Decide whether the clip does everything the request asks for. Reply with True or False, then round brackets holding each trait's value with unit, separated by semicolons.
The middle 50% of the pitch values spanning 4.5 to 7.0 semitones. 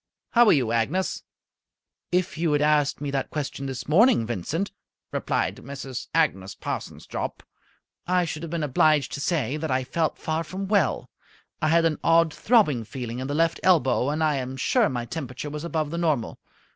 False (4.0 semitones)